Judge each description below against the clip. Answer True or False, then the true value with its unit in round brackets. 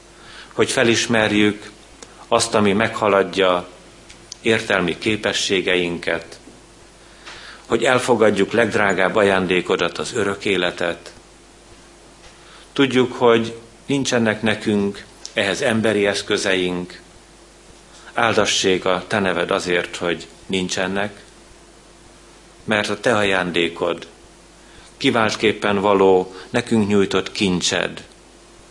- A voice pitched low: True (100 Hz)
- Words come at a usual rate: False (75 wpm)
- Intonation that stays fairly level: False (3.3 semitones)